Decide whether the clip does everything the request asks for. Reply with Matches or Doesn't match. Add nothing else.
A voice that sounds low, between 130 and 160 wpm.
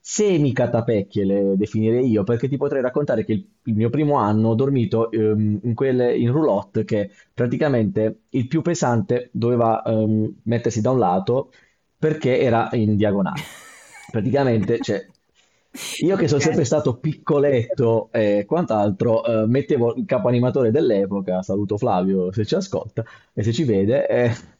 Matches